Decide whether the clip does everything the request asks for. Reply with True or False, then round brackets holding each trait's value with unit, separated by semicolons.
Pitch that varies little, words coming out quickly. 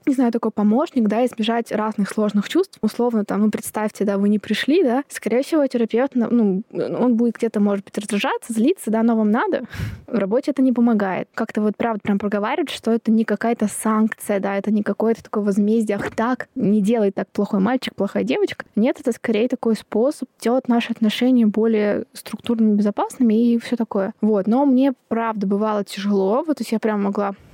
True (2.3 semitones; 195 wpm)